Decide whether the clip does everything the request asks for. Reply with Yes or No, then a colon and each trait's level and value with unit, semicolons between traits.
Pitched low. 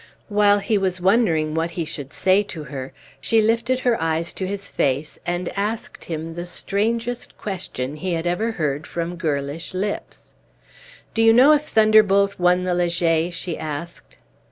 No: medium, 180 Hz